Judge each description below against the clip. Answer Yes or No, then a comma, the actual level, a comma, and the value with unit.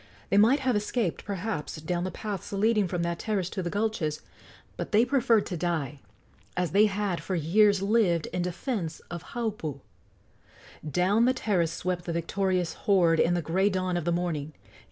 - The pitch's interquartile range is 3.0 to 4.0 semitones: Yes, average, 3.5 semitones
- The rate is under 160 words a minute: No, average, 175 wpm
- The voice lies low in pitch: No, medium, 185 Hz